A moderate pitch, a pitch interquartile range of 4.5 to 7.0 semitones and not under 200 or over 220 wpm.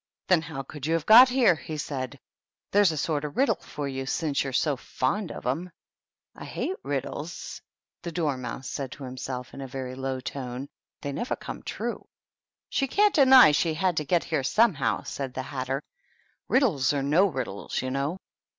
Yes: medium, 145 Hz; average, 5.1 semitones; fast, 205 wpm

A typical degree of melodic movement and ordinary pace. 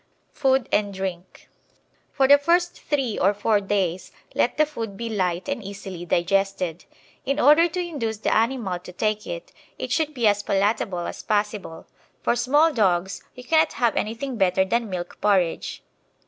No: wide, 5.9 semitones; average, 165 wpm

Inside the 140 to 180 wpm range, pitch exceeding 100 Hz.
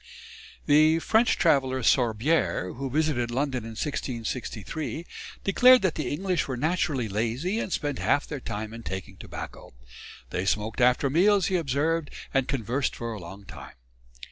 Yes: average, 150 wpm; low, 135 Hz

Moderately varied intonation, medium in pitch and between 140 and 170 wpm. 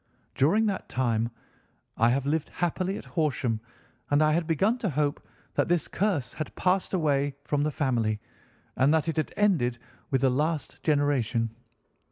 Yes: average, 4.4 semitones; medium, 145 Hz; average, 165 wpm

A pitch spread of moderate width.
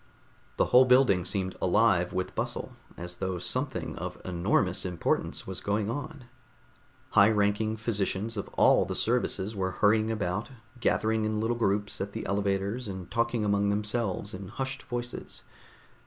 Yes: average, 3.0 semitones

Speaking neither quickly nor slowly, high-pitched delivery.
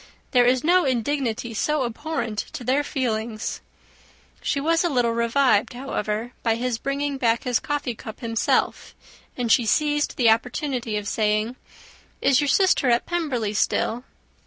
Yes: average, 150 wpm; high, 245 Hz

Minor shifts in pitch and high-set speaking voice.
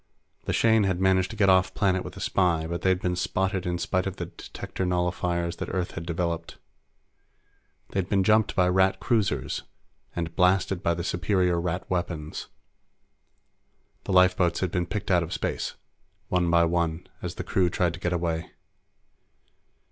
No: narrow, 1.6 semitones; very low, 90 Hz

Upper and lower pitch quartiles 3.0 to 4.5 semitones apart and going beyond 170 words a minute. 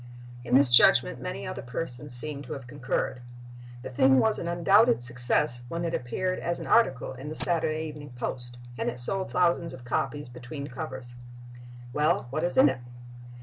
No: average, 5.1 semitones; average, 180 wpm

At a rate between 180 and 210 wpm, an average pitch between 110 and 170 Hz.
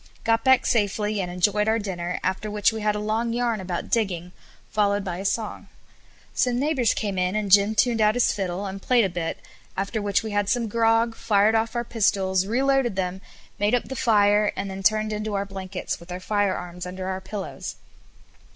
No: average, 200 wpm; high, 205 Hz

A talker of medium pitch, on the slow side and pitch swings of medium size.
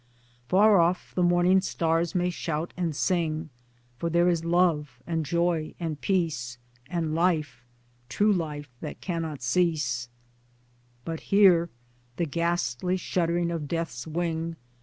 No: medium, 170 Hz; slow, 130 wpm; narrow, 2.2 semitones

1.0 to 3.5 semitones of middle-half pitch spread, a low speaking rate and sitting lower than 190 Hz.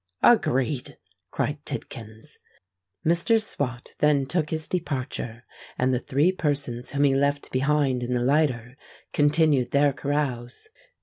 Yes: average, 3.1 semitones; slow, 125 wpm; medium, 140 Hz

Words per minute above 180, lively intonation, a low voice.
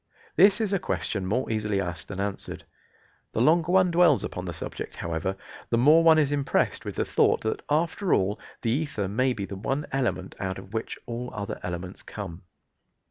Yes: average, 190 wpm; wide, 8.0 semitones; low, 115 Hz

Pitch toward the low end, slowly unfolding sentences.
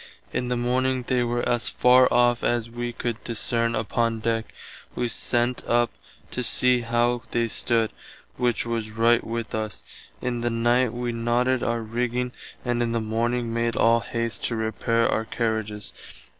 No: low, 120 Hz; average, 165 wpm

